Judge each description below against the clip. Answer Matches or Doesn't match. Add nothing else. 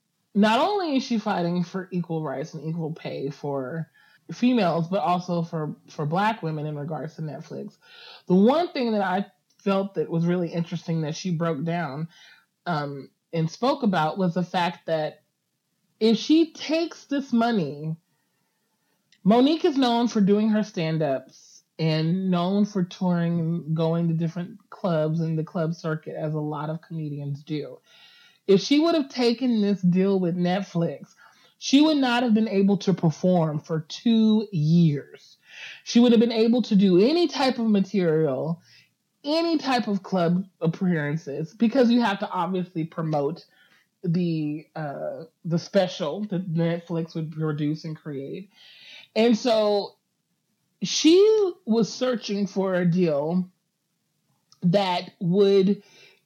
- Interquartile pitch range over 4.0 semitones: Matches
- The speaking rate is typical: Matches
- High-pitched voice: Doesn't match